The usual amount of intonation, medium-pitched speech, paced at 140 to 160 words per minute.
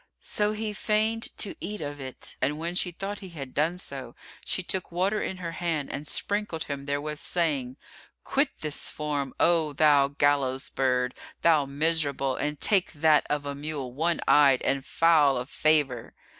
No: average, 3.8 semitones; medium, 150 Hz; average, 170 wpm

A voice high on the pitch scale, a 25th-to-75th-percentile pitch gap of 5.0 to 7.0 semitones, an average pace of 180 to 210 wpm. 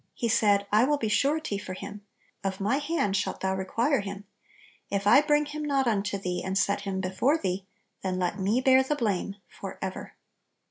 Yes: high, 205 Hz; wide, 5.6 semitones; average, 190 wpm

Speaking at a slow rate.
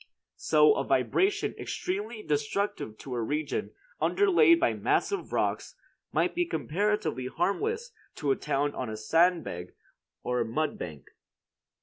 Yes: slow, 130 wpm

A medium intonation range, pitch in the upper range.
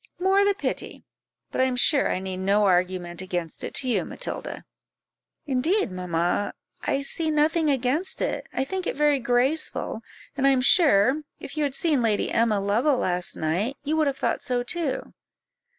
No: wide, 7.3 semitones; very high, 260 Hz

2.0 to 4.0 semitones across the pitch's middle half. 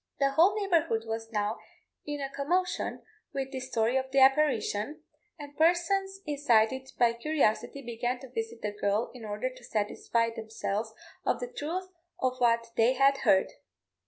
No: average, 4.6 semitones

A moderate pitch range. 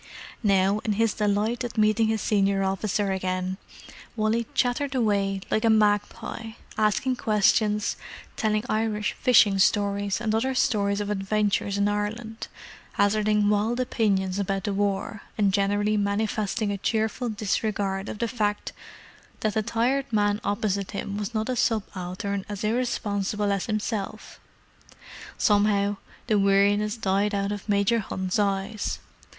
No: narrow, 1.6 semitones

